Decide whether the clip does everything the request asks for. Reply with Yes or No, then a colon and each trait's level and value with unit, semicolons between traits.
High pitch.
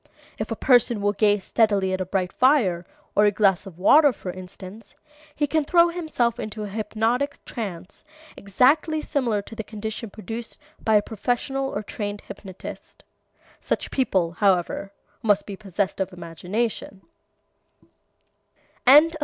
Yes: high, 210 Hz